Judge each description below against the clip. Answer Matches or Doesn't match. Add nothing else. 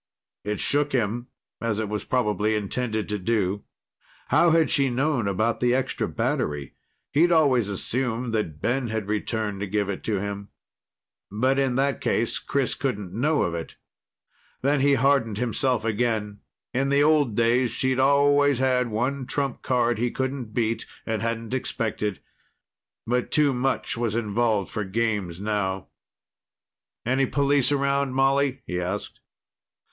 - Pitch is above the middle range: Doesn't match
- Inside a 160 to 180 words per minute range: Doesn't match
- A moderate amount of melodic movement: Matches